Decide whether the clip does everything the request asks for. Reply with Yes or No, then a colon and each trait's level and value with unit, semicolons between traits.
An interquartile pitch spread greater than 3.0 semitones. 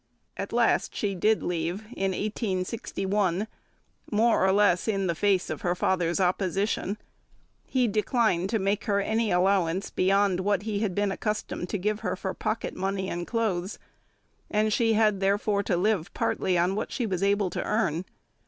No: narrow, 2.5 semitones